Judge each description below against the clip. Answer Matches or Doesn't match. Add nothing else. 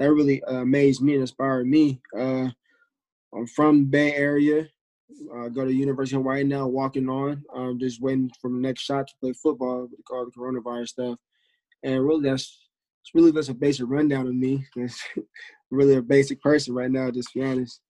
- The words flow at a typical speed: Matches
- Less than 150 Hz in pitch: Matches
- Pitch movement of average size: Doesn't match